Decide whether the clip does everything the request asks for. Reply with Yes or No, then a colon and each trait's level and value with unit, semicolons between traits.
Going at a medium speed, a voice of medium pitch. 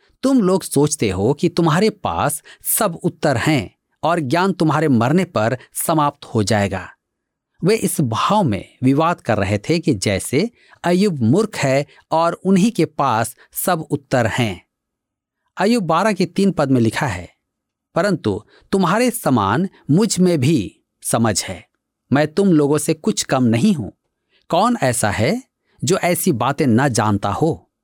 Yes: average, 155 wpm; medium, 155 Hz